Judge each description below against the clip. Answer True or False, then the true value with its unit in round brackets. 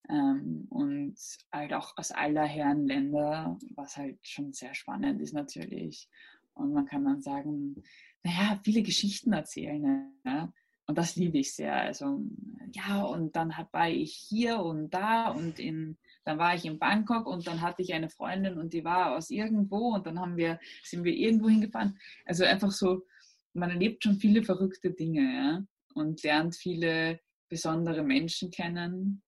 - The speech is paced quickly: False (170 wpm)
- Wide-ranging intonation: True (5.9 semitones)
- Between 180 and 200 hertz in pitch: True (185 Hz)